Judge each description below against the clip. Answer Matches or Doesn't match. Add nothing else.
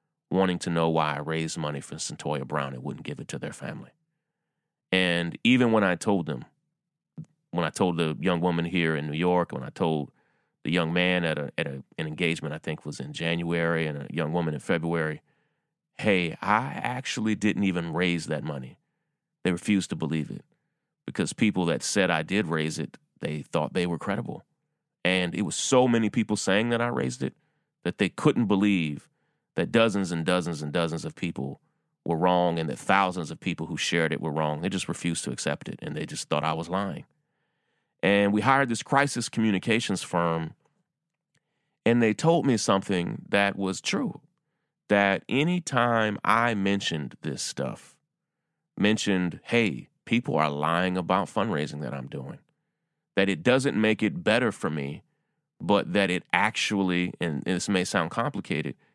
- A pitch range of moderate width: Doesn't match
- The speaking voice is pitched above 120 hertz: Doesn't match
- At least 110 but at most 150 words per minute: Doesn't match